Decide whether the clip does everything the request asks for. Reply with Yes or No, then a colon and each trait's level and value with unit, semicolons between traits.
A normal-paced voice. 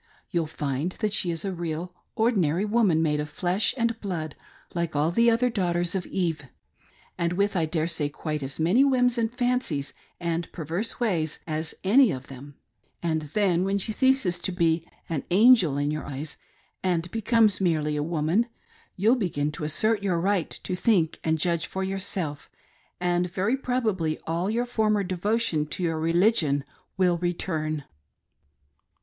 Yes: average, 165 wpm